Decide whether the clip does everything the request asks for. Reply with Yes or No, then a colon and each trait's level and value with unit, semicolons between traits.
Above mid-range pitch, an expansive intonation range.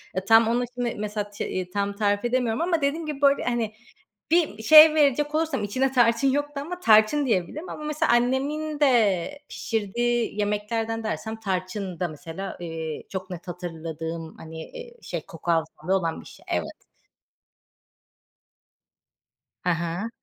Yes: high, 220 Hz; wide, 7.1 semitones